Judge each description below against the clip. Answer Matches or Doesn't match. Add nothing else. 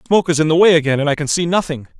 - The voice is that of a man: Matches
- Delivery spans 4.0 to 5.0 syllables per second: Doesn't match